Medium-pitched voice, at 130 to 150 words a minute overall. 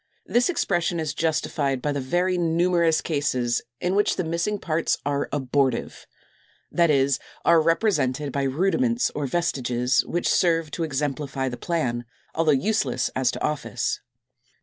Yes: medium, 155 Hz; average, 145 wpm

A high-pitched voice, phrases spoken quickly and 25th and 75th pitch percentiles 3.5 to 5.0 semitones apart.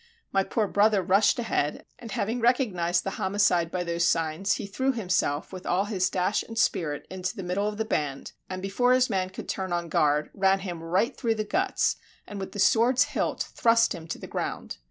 Yes: high, 195 Hz; fast, 210 wpm; average, 3.9 semitones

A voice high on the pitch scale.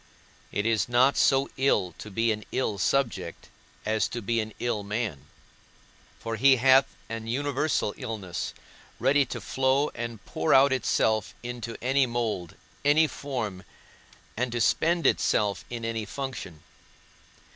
No: low, 115 Hz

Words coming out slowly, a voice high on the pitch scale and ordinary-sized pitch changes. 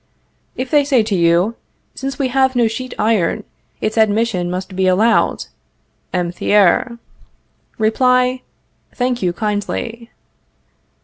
Yes: slow, 120 wpm; high, 225 Hz; average, 4.9 semitones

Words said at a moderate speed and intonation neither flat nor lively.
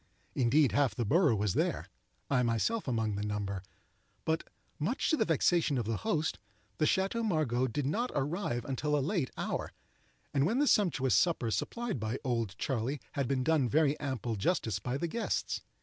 No: average, 170 wpm; wide, 6.0 semitones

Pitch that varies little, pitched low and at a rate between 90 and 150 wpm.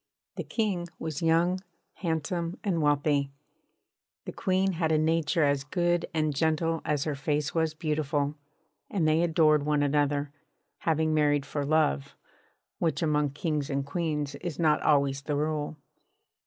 No: narrow, 2.2 semitones; medium, 155 Hz; average, 145 wpm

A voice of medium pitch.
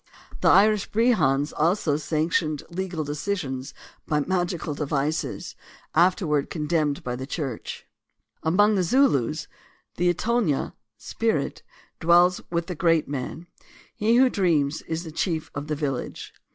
Yes: medium, 160 Hz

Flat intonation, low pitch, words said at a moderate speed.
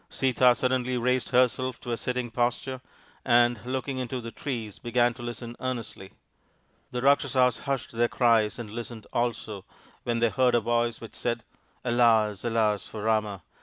Yes: narrow, 1.8 semitones; low, 120 Hz; average, 165 wpm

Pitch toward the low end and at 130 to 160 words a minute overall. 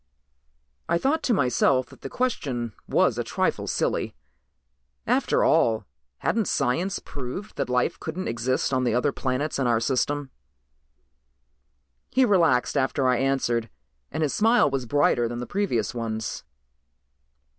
Yes: low, 130 Hz; average, 140 wpm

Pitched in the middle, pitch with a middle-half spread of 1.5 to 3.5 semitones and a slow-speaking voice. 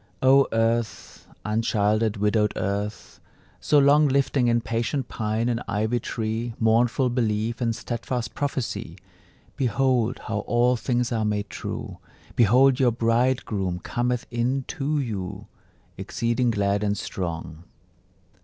No: low, 115 Hz; average, 2.8 semitones; slow, 120 wpm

